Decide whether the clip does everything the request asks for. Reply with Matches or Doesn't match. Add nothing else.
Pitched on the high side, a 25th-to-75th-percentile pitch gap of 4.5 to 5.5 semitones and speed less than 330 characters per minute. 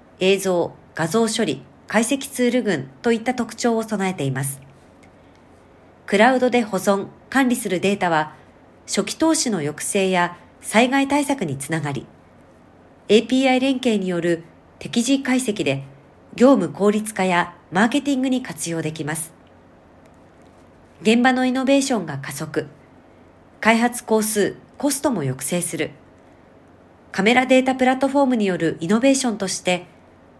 Doesn't match